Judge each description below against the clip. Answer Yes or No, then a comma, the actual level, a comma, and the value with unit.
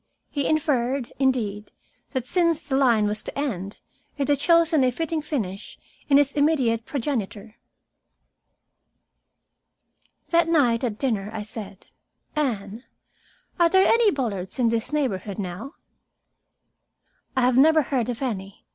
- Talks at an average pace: No, slow, 130 wpm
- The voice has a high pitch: Yes, very high, 255 Hz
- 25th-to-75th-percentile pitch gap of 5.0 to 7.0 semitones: Yes, wide, 5.4 semitones